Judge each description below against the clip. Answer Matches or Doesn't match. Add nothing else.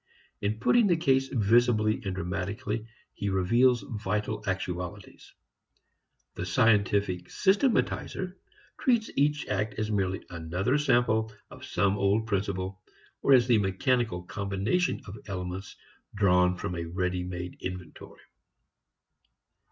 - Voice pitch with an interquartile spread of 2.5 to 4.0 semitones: Doesn't match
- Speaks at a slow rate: Matches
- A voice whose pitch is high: Doesn't match